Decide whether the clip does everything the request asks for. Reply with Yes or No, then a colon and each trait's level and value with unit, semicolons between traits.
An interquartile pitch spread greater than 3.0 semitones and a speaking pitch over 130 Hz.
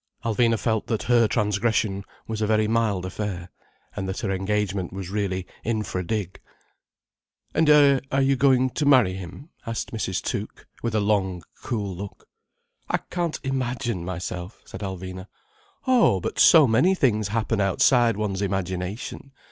No: average, 3.9 semitones; low, 105 Hz